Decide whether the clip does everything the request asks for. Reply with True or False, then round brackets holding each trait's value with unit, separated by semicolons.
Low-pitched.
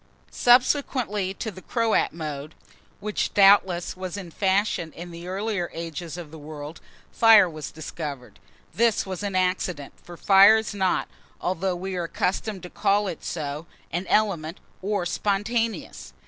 False (185 Hz)